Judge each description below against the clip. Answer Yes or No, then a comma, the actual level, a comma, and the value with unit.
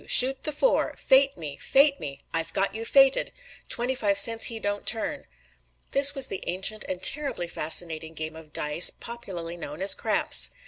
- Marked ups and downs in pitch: Yes, wide, 8.2 semitones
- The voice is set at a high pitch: Yes, high, 205 Hz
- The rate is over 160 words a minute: Yes, average, 175 wpm